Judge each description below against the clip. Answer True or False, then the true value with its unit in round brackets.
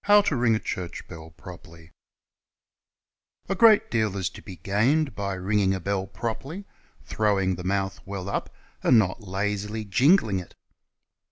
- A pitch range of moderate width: True (3.6 semitones)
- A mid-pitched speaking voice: False (100 Hz)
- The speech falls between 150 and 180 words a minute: False (140 wpm)